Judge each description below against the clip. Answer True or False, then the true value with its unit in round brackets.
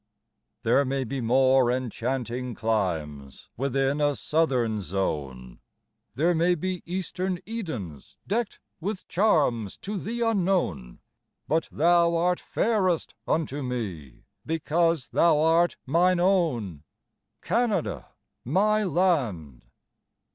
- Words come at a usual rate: False (105 wpm)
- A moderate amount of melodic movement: False (7.6 semitones)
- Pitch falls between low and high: True (145 Hz)